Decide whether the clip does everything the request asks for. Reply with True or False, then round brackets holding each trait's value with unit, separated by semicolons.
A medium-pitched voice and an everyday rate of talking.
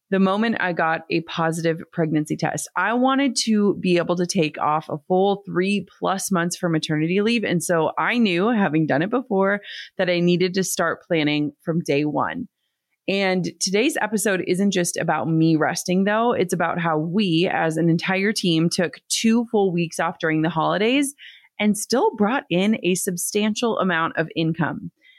True (180 Hz; 180 wpm)